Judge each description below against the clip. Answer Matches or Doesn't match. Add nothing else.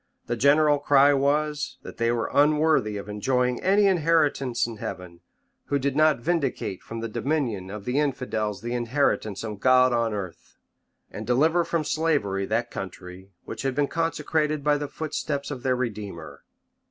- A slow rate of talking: Doesn't match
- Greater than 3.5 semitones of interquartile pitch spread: Matches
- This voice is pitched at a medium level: Doesn't match